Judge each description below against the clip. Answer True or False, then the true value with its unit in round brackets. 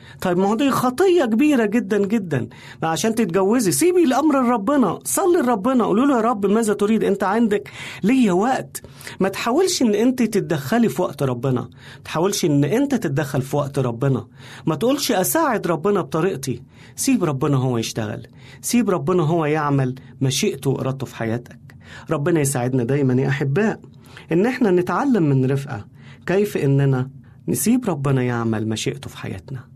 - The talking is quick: True (150 wpm)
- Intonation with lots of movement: True (8.9 semitones)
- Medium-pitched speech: True (160 Hz)